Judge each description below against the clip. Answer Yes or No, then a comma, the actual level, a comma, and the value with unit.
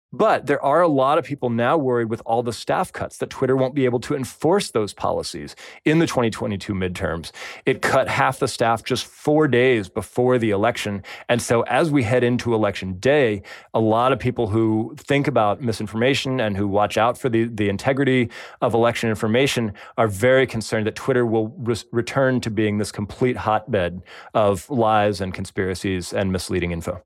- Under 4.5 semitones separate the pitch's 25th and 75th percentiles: Yes, average, 3.3 semitones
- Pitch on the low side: Yes, low, 115 Hz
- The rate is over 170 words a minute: Yes, average, 190 wpm